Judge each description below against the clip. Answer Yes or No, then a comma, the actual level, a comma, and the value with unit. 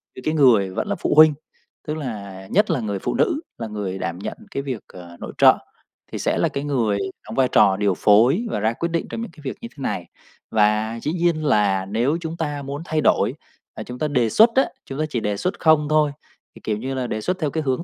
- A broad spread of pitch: Yes, wide, 6.7 semitones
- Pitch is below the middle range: Yes, low, 130 Hz